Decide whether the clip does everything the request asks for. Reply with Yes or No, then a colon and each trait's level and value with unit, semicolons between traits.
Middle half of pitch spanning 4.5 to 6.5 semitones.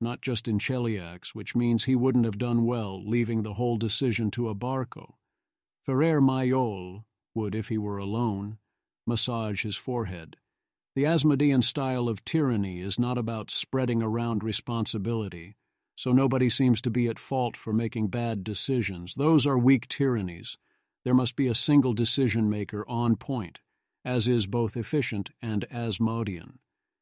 No: average, 2.9 semitones